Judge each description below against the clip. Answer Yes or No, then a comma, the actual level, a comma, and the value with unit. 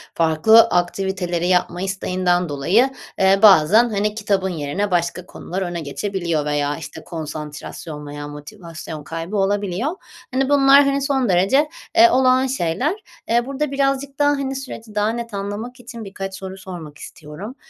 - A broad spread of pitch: Yes, wide, 6.4 semitones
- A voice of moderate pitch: No, high, 195 Hz